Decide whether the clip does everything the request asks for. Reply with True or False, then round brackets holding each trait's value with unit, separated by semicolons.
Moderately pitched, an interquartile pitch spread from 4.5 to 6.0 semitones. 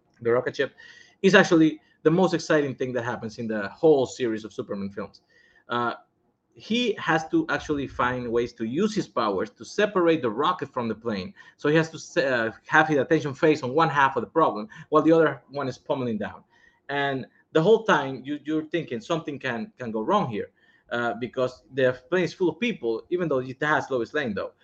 True (150 Hz; 5.1 semitones)